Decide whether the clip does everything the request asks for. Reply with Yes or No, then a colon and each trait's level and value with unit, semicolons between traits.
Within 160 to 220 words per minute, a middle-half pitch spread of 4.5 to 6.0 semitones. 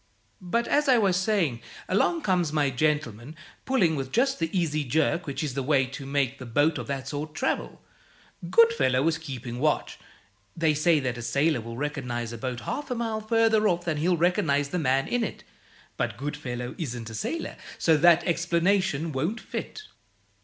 Yes: average, 180 wpm; wide, 5.5 semitones